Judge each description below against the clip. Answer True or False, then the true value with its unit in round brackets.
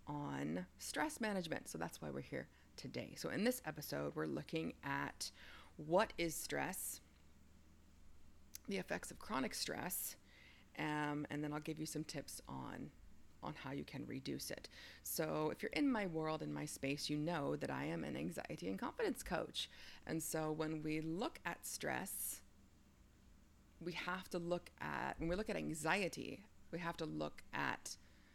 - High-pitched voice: False (140 Hz)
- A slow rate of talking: False (170 wpm)